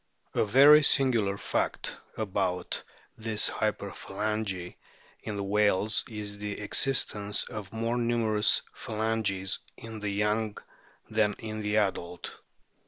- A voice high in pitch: No, low, 105 Hz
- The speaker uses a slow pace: Yes, slow, 110 wpm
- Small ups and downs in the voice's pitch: Yes, narrow, 1.7 semitones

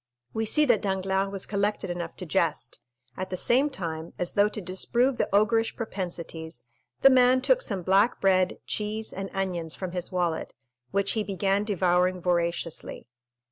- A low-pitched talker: No, high, 195 Hz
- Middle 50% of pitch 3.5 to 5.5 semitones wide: No, average, 3.1 semitones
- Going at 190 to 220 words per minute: No, average, 165 wpm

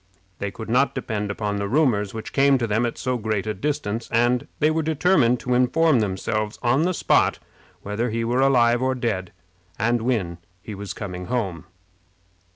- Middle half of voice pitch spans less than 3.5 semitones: No, average, 3.8 semitones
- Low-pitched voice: Yes, low, 115 Hz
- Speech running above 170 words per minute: Yes, average, 180 wpm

